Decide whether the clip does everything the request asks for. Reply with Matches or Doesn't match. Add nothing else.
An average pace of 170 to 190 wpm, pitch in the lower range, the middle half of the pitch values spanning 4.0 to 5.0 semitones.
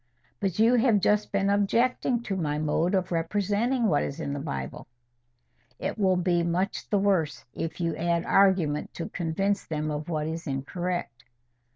Doesn't match